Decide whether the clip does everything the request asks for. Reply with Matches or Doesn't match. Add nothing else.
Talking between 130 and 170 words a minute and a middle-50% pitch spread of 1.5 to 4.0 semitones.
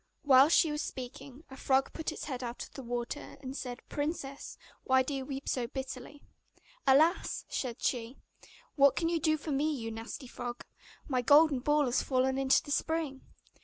Doesn't match